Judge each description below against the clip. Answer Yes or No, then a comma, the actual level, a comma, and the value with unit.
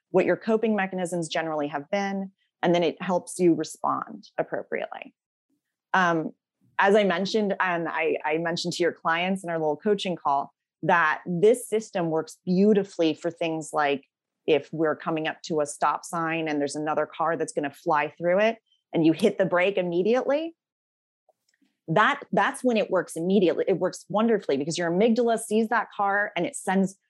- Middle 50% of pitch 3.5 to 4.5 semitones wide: Yes, average, 4.1 semitones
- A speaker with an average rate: Yes, average, 175 wpm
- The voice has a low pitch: No, medium, 175 Hz